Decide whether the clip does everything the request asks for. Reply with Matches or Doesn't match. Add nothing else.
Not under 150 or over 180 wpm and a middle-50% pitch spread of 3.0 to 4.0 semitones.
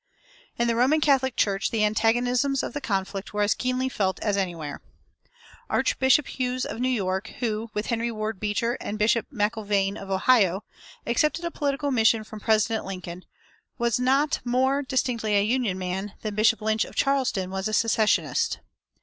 Matches